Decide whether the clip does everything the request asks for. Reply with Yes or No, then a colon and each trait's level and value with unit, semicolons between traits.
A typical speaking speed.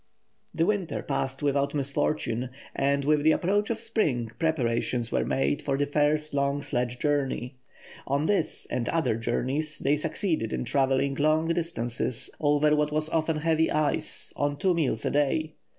Yes: average, 160 wpm